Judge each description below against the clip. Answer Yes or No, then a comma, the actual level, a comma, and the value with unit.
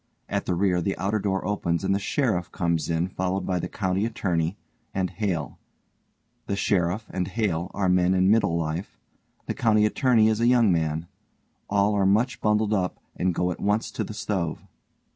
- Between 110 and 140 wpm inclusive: No, average, 185 wpm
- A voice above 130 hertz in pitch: No, very low, 95 Hz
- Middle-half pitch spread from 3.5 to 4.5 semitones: No, average, 3.1 semitones